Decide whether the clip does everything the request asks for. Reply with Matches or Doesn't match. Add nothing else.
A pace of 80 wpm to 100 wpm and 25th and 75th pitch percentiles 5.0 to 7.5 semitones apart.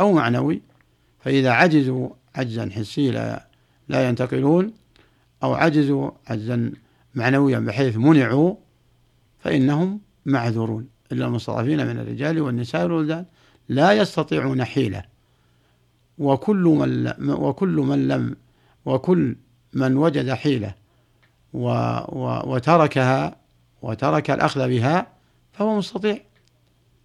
Matches